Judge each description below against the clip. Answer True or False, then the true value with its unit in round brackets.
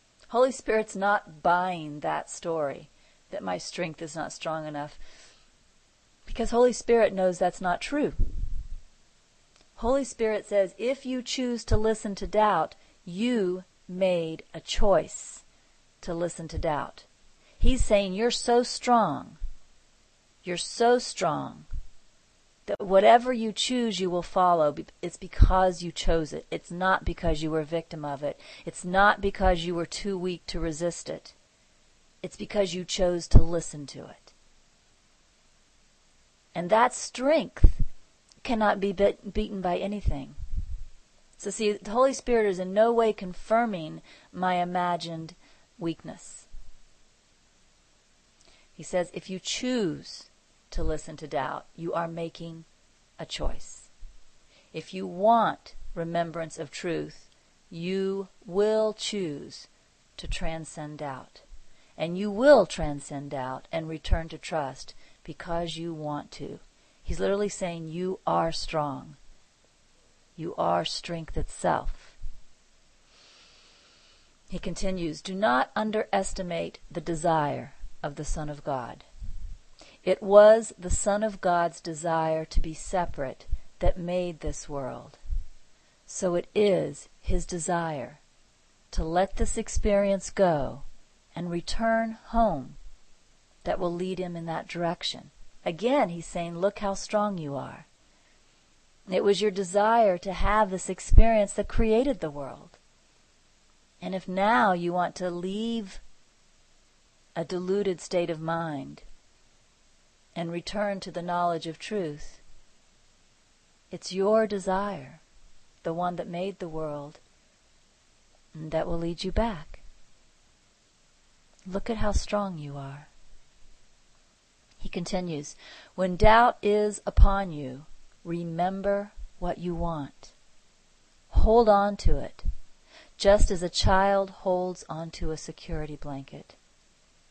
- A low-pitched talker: False (180 Hz)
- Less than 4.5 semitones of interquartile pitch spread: True (3.8 semitones)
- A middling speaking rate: False (125 wpm)